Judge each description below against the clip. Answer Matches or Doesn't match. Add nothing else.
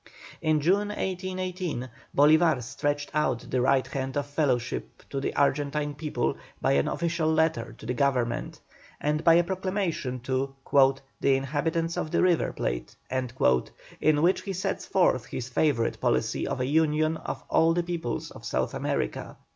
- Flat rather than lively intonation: Doesn't match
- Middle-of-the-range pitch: Matches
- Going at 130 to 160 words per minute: Matches